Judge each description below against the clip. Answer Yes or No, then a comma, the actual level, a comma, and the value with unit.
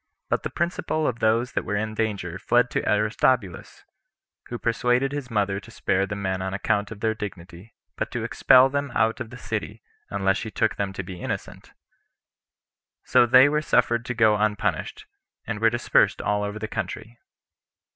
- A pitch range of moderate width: Yes, average, 3.2 semitones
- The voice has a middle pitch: No, low, 110 Hz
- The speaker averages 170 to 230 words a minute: Yes, average, 180 wpm